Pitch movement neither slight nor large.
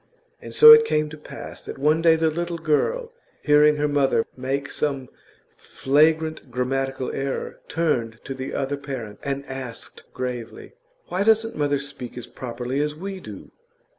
Yes: average, 3.2 semitones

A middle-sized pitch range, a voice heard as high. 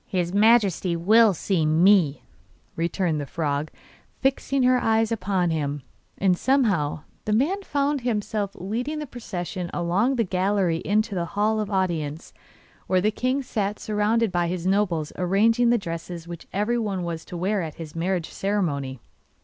Yes: average, 4.6 semitones; high, 195 Hz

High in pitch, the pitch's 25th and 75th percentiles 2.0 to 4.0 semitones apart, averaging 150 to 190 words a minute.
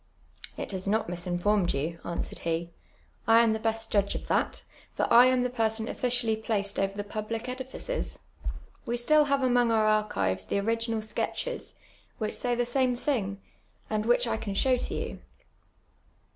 Yes: high, 225 Hz; average, 3.4 semitones; average, 170 wpm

